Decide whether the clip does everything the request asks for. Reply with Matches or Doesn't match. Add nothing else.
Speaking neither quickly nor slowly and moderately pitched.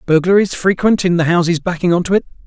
Doesn't match